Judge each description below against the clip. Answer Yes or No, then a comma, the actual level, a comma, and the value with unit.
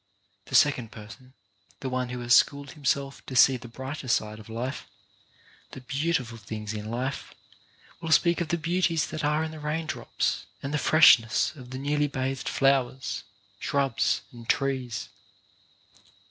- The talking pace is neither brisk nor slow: Yes, average, 160 wpm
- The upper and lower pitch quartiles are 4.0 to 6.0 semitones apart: No, average, 3.5 semitones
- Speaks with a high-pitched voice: No, low, 135 Hz